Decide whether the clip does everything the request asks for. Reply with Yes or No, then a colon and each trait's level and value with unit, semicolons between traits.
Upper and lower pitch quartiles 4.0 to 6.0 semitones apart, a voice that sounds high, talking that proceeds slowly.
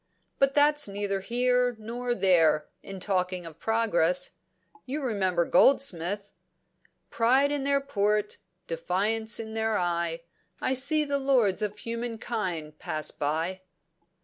Yes: wide, 5.5 semitones; high, 210 Hz; slow, 125 wpm